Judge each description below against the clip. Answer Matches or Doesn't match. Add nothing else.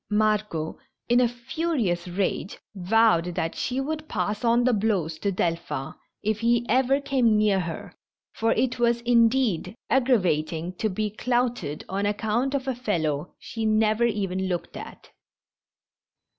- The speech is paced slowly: Doesn't match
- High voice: Matches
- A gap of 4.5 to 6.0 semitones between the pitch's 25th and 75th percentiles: Matches